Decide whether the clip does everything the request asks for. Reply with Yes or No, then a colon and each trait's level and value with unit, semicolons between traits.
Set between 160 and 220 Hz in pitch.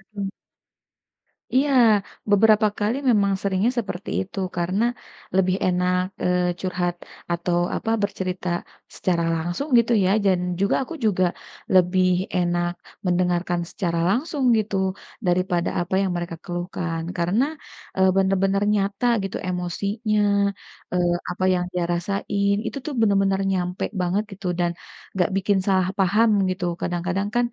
Yes: medium, 185 Hz